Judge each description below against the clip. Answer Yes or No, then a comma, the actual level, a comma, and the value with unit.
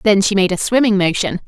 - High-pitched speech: Yes, high, 200 Hz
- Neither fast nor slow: No, fast, 245 wpm